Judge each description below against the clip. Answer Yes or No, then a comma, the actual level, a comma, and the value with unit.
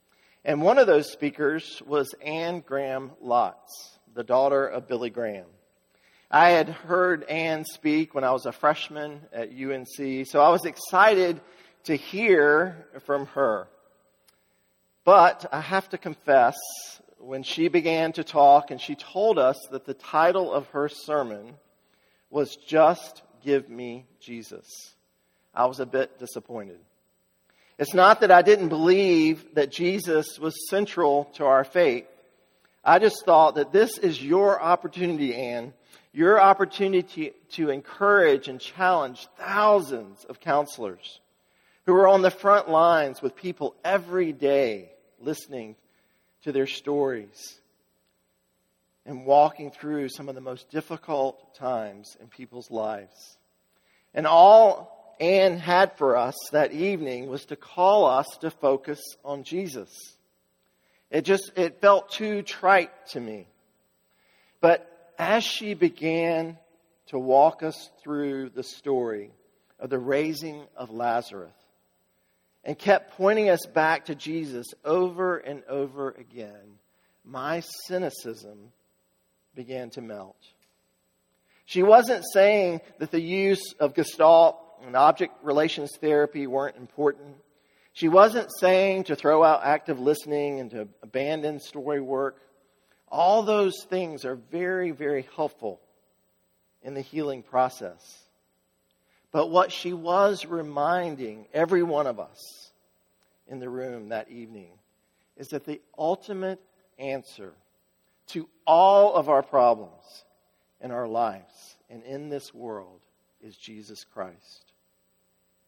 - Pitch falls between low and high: Yes, medium, 145 Hz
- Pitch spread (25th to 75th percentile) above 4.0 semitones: Yes, average, 5.1 semitones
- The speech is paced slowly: Yes, slow, 130 wpm